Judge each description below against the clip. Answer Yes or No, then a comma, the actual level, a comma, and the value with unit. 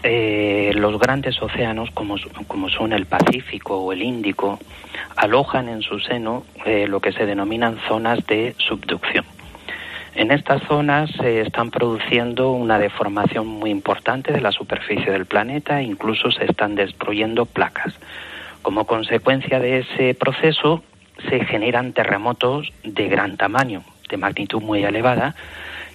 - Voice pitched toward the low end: Yes, low, 115 Hz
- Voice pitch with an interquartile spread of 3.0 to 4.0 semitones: Yes, average, 3.6 semitones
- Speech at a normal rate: Yes, average, 140 wpm